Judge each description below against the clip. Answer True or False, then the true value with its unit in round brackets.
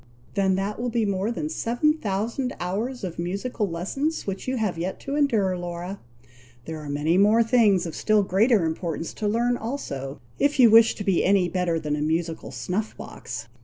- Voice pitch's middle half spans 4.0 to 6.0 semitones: True (5.2 semitones)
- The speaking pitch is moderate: False (200 Hz)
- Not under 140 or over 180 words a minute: False (190 wpm)